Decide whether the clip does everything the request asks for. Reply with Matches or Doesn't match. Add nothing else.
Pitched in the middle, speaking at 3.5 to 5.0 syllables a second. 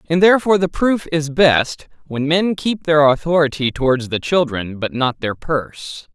Matches